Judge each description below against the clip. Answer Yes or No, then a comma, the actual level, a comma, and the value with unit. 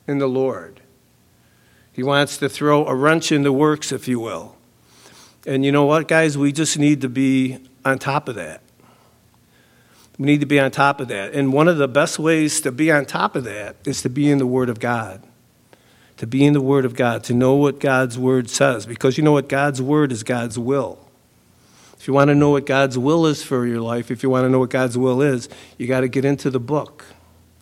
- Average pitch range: No, narrow, 2.0 semitones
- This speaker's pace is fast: Yes, fast, 230 wpm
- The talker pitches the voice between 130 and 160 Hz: Yes, low, 135 Hz